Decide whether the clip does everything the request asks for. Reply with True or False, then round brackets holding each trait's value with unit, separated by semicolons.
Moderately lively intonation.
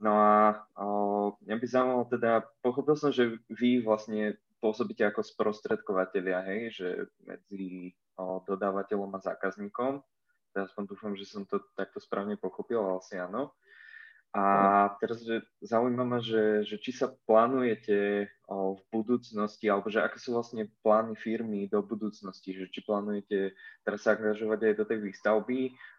False (2.3 semitones)